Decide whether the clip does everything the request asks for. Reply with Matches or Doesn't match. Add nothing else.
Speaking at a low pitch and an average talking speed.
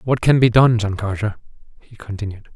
Matches